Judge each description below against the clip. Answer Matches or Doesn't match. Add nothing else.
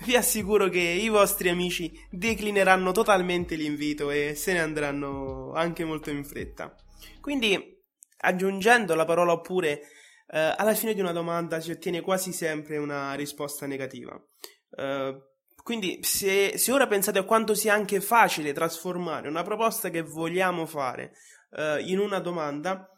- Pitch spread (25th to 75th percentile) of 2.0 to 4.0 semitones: Doesn't match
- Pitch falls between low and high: Matches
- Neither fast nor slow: Matches